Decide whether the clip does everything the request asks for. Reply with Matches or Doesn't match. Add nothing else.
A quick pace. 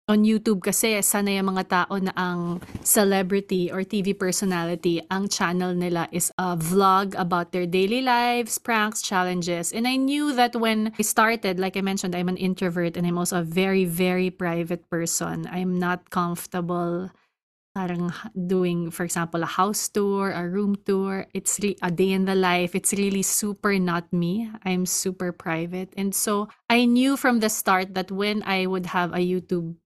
Matches